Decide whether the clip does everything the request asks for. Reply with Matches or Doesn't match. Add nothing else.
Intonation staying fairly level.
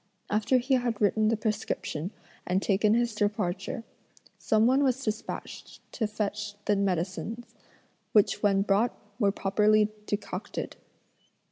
Matches